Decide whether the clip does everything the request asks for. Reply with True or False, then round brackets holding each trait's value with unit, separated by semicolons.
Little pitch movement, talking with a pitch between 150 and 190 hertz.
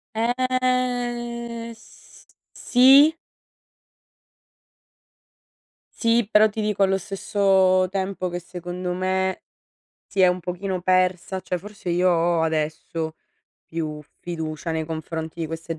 False (4.3 semitones; 185 Hz)